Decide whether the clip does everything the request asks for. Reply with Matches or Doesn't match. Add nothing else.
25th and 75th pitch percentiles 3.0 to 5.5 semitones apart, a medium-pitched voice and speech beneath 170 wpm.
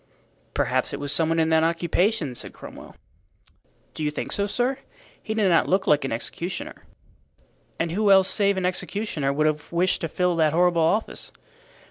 Doesn't match